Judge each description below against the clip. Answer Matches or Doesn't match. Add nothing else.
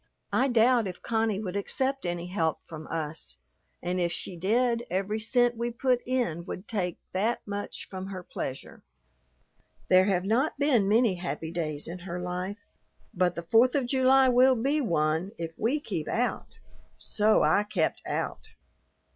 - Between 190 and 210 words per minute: Doesn't match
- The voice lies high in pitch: Matches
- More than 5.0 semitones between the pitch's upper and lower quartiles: Matches